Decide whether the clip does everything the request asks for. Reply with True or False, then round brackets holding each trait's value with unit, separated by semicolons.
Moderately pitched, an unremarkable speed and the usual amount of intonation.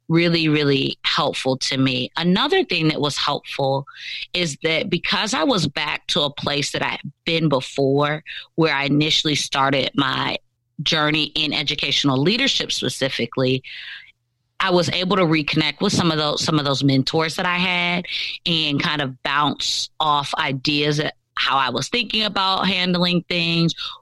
True (155 Hz; 160 wpm; 4.0 semitones)